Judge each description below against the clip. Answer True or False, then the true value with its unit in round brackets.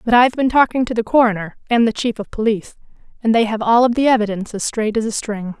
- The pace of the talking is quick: True (255 wpm)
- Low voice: False (225 Hz)